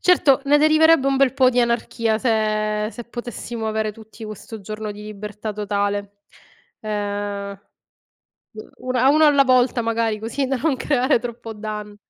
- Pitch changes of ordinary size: Yes, average, 3.3 semitones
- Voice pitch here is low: No, high, 225 Hz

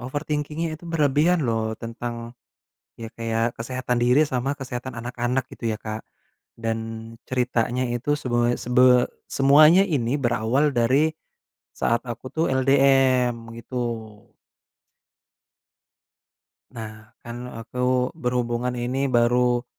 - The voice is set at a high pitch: No, low, 125 Hz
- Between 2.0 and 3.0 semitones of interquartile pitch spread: Yes, narrow, 2.4 semitones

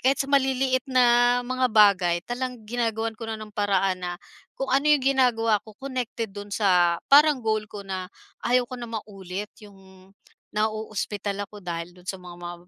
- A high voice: Yes, high, 220 Hz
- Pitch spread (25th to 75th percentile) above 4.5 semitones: No, average, 4.2 semitones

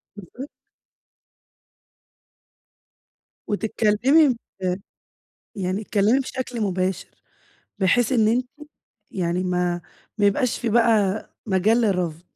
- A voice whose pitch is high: Yes, high, 210 Hz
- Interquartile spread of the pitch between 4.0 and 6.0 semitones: Yes, average, 4.3 semitones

